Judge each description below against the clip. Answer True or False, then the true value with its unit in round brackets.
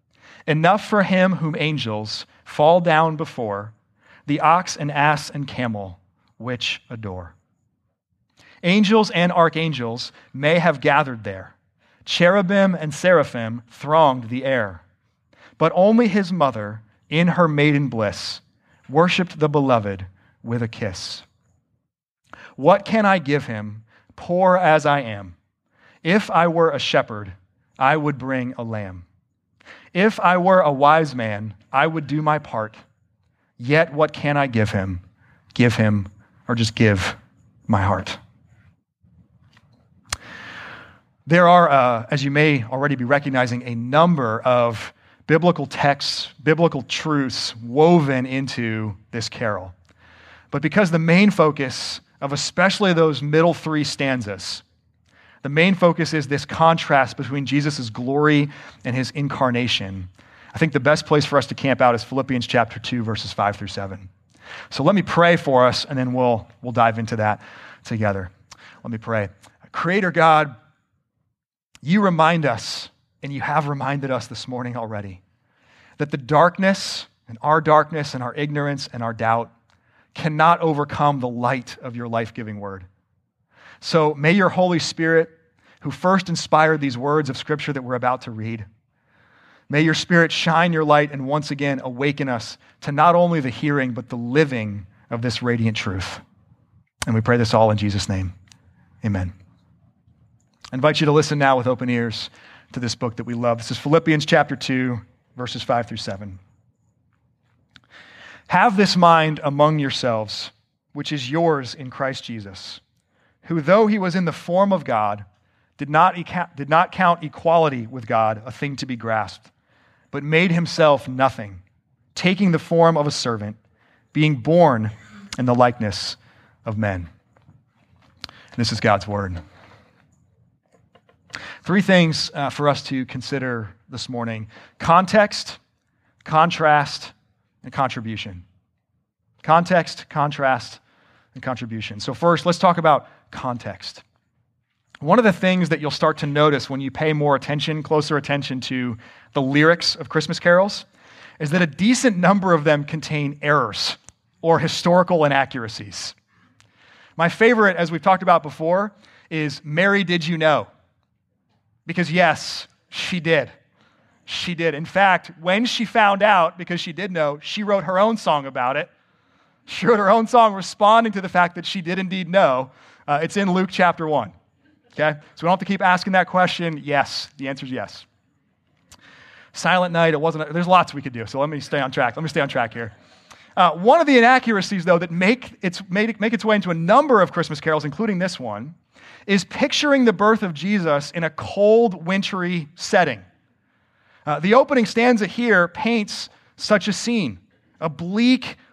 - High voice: False (140 Hz)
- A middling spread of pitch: False (6.3 semitones)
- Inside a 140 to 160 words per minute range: True (155 wpm)